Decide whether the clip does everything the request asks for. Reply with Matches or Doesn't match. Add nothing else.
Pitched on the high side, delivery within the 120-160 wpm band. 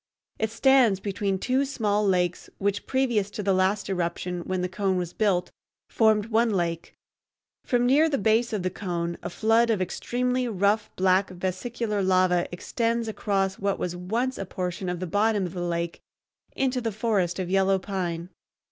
Doesn't match